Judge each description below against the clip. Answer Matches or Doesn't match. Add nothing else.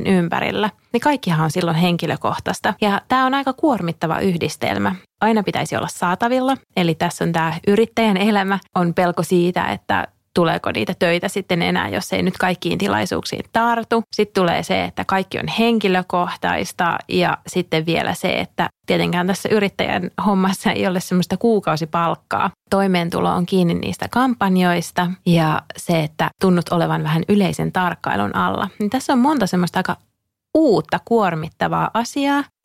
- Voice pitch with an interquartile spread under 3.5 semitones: Doesn't match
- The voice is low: Doesn't match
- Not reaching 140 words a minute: Doesn't match